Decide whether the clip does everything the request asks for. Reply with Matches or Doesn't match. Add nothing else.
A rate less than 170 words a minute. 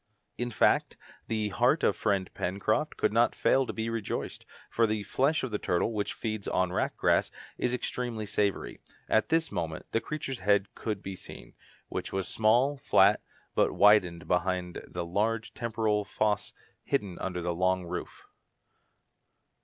Matches